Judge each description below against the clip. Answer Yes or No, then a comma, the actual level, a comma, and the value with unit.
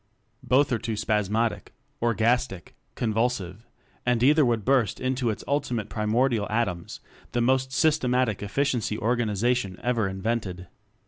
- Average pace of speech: No, slow, 125 wpm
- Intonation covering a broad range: No, average, 3.0 semitones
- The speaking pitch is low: Yes, low, 115 Hz